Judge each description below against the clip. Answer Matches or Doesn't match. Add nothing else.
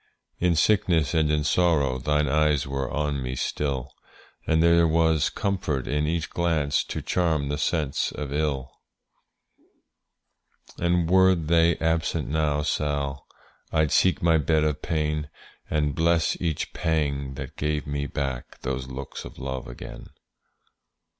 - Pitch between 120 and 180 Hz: Doesn't match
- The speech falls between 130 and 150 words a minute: Matches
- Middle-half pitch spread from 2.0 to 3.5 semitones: Matches